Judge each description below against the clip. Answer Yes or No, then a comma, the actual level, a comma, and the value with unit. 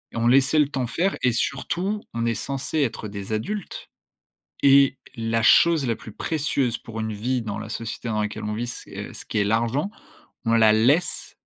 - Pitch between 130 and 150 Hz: No, low, 120 Hz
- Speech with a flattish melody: No, average, 4.0 semitones